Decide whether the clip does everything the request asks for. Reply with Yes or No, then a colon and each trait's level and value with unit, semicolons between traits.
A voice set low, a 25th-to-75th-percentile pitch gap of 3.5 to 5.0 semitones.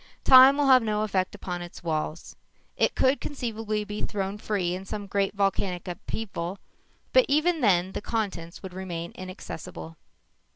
No: high, 200 Hz; average, 3.9 semitones